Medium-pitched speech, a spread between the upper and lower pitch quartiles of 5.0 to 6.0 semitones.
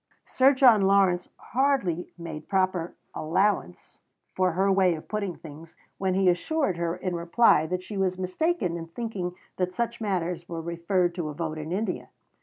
No: medium, 180 Hz; average, 2.9 semitones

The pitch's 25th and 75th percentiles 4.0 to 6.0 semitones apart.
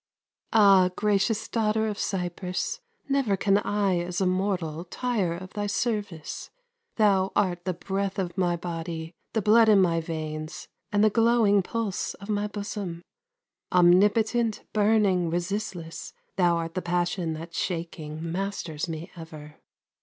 No: average, 3.4 semitones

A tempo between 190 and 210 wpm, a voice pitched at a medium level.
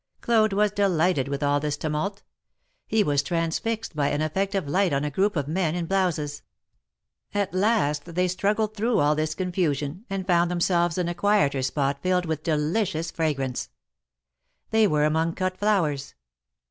No: average, 170 wpm; medium, 170 Hz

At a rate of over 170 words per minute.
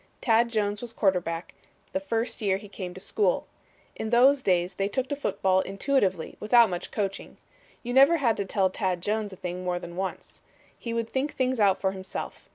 Yes: average, 195 wpm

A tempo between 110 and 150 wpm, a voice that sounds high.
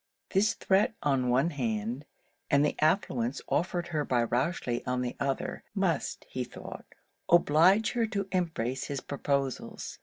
No: average, 145 wpm; medium, 145 Hz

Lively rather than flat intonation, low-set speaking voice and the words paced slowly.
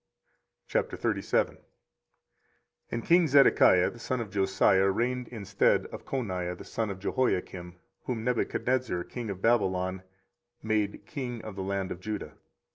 No: average, 4.4 semitones; low, 105 Hz; slow, 130 wpm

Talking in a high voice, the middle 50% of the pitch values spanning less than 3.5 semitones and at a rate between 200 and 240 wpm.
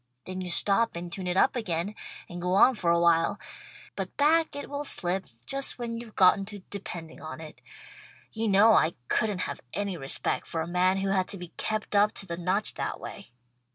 No: high, 195 Hz; average, 3.8 semitones; fast, 205 wpm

